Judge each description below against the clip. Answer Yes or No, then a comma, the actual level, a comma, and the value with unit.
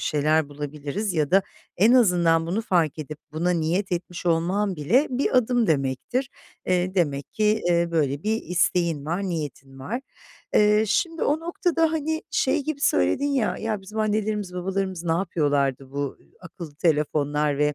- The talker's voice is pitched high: No, medium, 180 Hz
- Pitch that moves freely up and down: Yes, wide, 6.2 semitones